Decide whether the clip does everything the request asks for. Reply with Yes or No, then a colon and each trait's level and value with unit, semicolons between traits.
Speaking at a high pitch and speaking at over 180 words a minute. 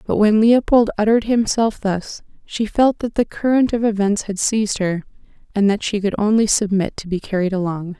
Yes: high, 210 Hz; average, 195 wpm